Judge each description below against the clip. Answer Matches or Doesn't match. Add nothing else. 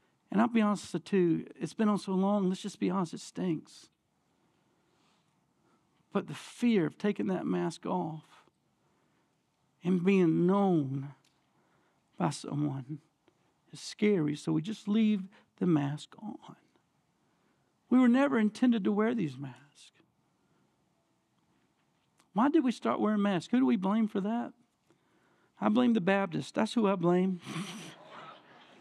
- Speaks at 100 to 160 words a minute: Matches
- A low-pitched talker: Doesn't match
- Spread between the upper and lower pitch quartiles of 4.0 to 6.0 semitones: Matches